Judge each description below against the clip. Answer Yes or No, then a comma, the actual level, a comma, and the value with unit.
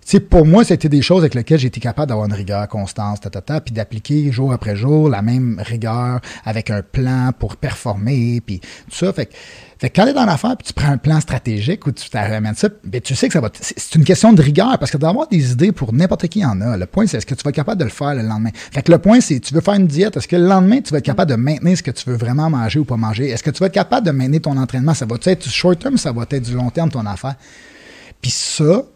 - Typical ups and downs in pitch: No, wide, 5.9 semitones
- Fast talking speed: Yes, fast, 300 wpm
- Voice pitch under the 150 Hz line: Yes, medium, 140 Hz